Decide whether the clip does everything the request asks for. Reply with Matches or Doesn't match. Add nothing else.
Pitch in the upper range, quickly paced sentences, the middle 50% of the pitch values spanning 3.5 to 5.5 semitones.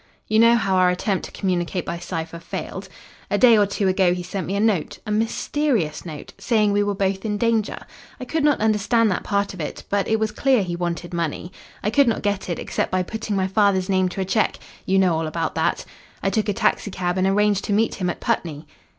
Doesn't match